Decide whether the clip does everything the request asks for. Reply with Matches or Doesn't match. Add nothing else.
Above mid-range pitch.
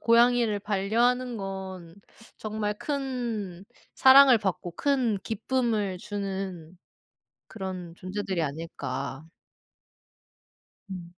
Matches